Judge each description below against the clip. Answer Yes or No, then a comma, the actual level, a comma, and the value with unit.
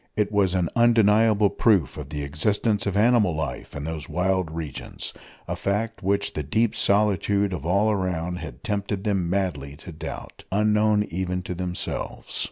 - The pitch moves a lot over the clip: No, average, 3.7 semitones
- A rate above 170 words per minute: No, average, 165 wpm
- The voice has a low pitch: Yes, very low, 95 Hz